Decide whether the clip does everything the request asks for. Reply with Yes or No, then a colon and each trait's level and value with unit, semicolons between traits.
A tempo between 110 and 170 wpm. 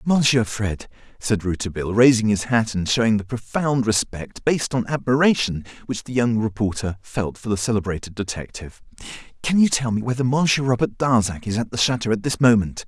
No: average, 180 wpm